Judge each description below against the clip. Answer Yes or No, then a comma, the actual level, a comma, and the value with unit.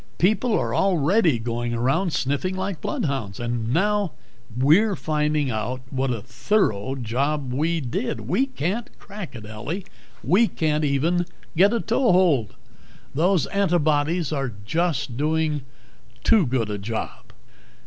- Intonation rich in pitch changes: Yes, wide, 6.7 semitones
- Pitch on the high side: No, medium, 150 Hz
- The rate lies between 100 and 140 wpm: Yes, slow, 135 wpm